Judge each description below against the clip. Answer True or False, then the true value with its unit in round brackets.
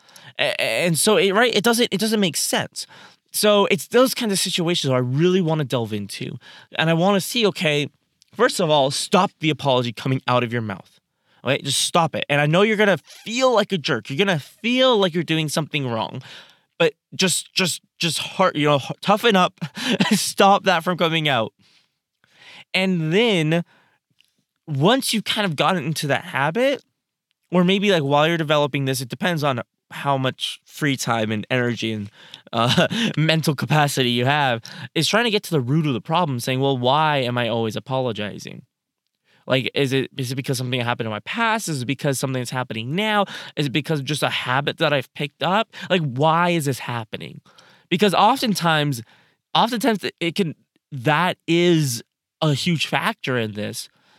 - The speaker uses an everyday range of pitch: False (6.0 semitones)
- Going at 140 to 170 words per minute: False (185 wpm)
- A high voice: False (155 Hz)